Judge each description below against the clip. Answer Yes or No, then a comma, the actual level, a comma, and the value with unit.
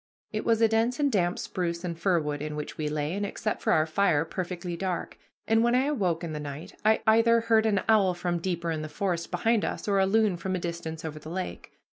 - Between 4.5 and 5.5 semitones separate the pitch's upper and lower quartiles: Yes, average, 4.8 semitones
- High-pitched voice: No, medium, 180 Hz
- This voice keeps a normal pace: No, fast, 245 wpm